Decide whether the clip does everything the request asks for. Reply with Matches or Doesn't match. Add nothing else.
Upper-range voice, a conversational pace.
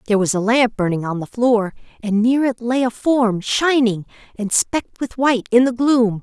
Doesn't match